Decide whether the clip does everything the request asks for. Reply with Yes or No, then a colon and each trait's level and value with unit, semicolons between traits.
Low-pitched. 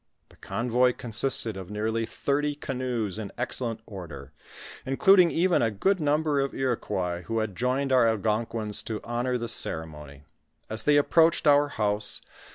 Yes: low, 120 Hz